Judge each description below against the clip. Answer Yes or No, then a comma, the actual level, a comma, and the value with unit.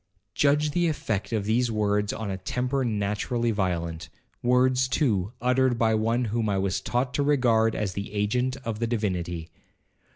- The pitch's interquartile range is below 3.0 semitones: No, average, 3.6 semitones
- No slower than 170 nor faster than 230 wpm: No, average, 160 wpm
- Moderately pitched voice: No, low, 115 Hz